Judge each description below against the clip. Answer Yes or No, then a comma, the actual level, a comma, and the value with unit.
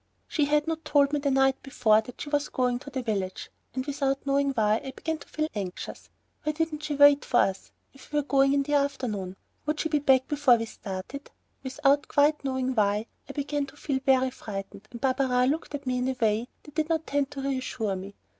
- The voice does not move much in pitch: No, average, 3.1 semitones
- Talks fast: Yes, fast, 225 wpm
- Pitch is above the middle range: Yes, very high, 270 Hz